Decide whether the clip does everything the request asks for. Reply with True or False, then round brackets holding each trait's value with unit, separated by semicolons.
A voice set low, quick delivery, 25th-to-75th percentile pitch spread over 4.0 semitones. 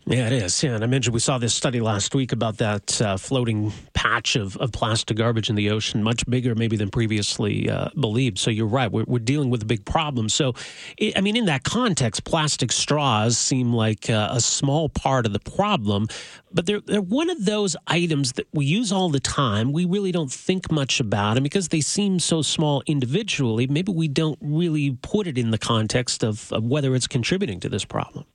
True (130 Hz; 220 wpm; 5.5 semitones)